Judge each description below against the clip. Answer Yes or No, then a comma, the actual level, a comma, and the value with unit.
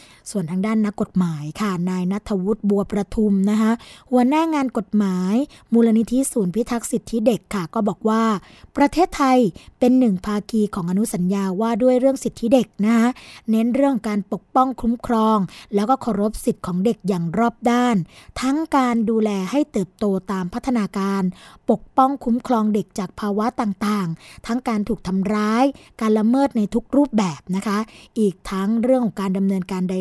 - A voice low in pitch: No, high, 220 Hz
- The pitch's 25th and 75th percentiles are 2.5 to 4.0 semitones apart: Yes, average, 3.4 semitones